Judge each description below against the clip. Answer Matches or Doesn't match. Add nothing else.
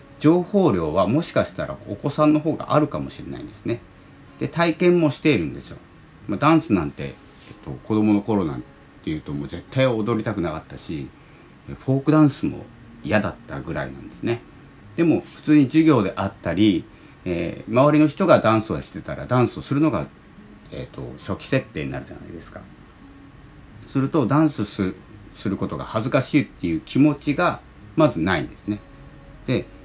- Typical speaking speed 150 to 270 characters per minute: Doesn't match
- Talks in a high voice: Doesn't match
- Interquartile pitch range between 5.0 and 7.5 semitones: Matches